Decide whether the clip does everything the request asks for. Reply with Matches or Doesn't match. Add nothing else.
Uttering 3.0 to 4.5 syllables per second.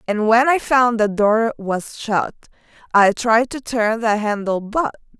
Matches